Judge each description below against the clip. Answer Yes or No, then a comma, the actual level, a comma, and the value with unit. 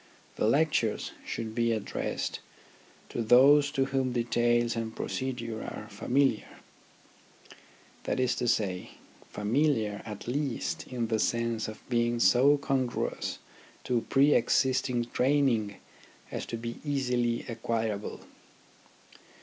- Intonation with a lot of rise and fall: No, average, 2.8 semitones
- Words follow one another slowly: Yes, slow, 115 wpm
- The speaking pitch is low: Yes, low, 120 Hz